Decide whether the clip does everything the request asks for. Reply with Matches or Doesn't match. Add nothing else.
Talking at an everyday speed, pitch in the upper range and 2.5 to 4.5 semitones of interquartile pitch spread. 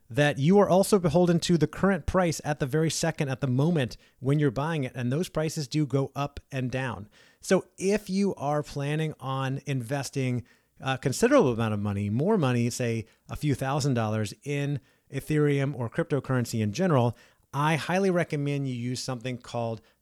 Doesn't match